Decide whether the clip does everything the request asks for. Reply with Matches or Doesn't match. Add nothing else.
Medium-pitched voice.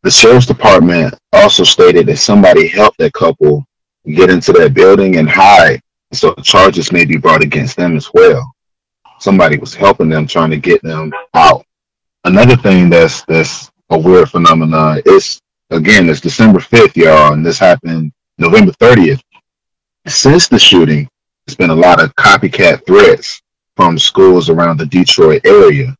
Doesn't match